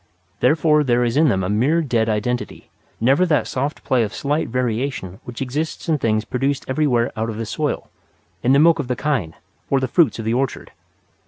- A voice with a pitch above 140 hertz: No, low, 130 Hz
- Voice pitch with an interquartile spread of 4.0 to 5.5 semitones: Yes, average, 4.3 semitones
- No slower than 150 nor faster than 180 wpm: No, average, 200 wpm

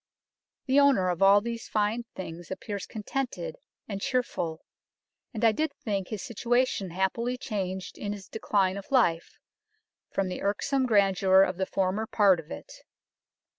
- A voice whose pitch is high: Yes, high, 205 Hz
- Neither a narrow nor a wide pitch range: Yes, average, 3.9 semitones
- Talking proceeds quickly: No, average, 155 wpm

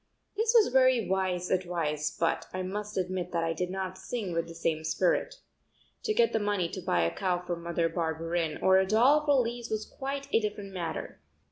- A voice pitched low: No, medium, 185 Hz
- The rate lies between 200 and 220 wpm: Yes, fast, 205 wpm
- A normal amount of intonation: Yes, average, 4.8 semitones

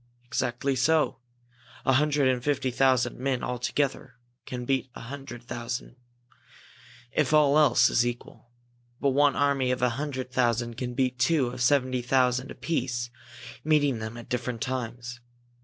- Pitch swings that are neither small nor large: No, narrow, 2.3 semitones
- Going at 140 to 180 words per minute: Yes, average, 155 wpm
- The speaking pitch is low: Yes, low, 130 Hz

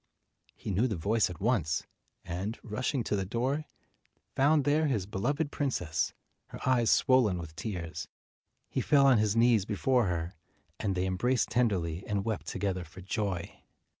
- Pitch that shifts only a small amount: No, wide, 5.6 semitones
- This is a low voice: Yes, low, 105 Hz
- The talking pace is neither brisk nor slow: Yes, average, 160 wpm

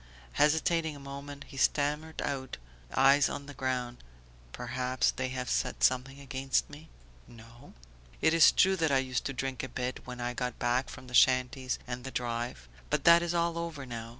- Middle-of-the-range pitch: No, low, 130 Hz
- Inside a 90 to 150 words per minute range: No, average, 185 wpm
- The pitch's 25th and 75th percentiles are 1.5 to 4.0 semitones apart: Yes, narrow, 2.6 semitones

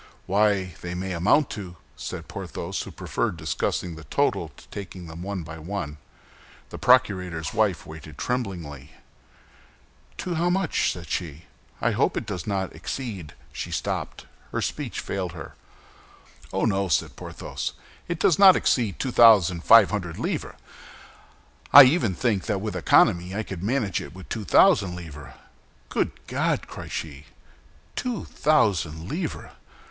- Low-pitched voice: Yes, very low, 95 Hz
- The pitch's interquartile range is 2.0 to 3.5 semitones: No, average, 4.8 semitones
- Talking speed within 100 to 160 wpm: Yes, average, 145 wpm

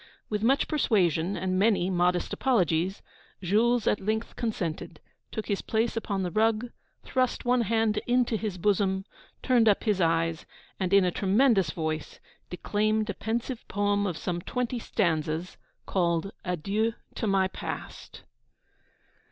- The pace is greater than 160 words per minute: No, average, 140 wpm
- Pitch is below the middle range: No, high, 200 Hz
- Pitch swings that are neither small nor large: Yes, average, 3.9 semitones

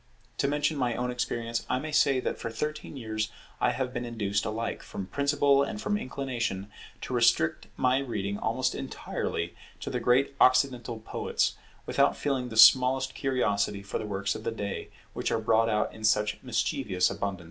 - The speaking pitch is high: No, low, 120 Hz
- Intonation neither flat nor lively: Yes, average, 3.7 semitones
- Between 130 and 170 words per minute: No, average, 180 wpm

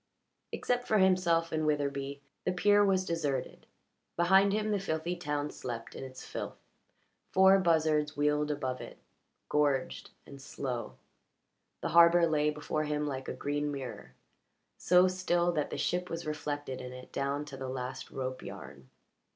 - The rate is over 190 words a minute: No, average, 155 wpm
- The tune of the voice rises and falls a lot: No, average, 4.0 semitones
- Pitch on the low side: No, medium, 150 Hz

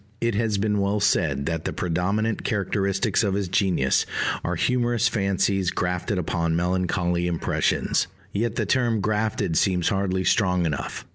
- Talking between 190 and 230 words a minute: No, average, 145 wpm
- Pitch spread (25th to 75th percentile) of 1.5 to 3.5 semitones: Yes, average, 3.1 semitones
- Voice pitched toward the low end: Yes, very low, 95 Hz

